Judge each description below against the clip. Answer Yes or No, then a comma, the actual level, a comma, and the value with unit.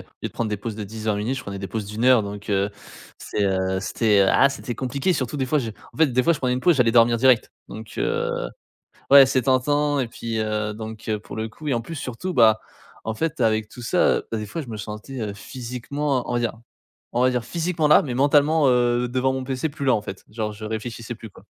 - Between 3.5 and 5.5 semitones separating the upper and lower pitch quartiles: Yes, average, 3.8 semitones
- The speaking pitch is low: Yes, low, 120 Hz